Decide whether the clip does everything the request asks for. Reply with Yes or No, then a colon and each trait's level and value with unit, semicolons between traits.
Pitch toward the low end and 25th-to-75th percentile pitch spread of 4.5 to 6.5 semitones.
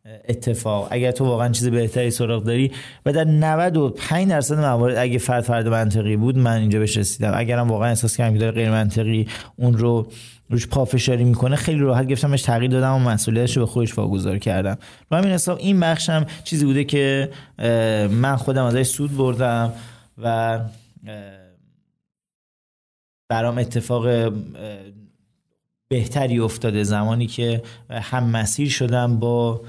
No: low, 120 Hz; narrow, 2.6 semitones